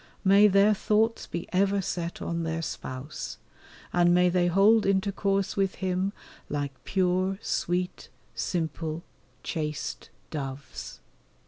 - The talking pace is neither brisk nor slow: No, slow, 115 wpm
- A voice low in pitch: No, medium, 180 Hz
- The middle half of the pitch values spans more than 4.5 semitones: No, average, 3.1 semitones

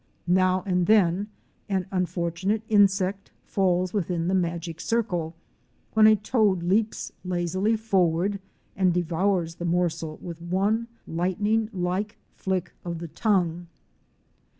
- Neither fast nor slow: No, slow, 125 wpm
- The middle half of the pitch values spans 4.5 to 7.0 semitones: No, average, 2.8 semitones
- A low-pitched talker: No, medium, 185 Hz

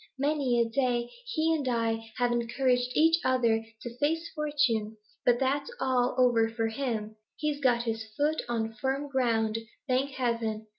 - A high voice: Yes, high, 245 Hz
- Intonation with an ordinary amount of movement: Yes, average, 3.5 semitones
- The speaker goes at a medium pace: Yes, average, 155 wpm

